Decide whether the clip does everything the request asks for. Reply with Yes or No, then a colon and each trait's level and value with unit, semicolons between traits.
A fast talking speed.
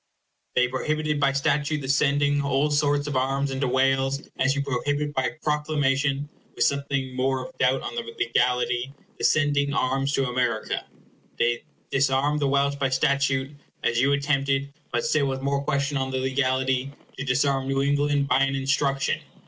No: average, 165 wpm